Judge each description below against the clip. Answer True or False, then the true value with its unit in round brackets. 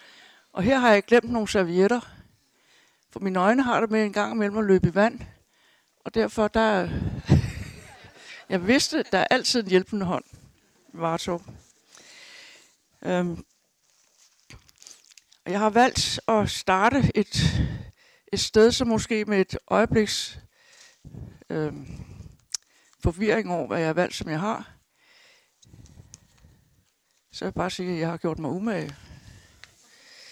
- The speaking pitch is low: False (215 Hz)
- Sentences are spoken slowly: True (135 wpm)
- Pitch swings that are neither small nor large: True (4.4 semitones)